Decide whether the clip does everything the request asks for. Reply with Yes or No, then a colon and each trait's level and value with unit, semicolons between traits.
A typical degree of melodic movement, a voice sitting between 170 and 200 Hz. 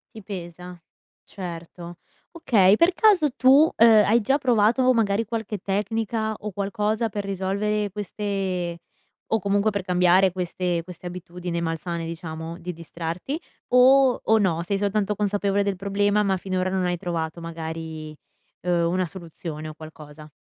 Yes: average, 3.5 semitones; high, 190 Hz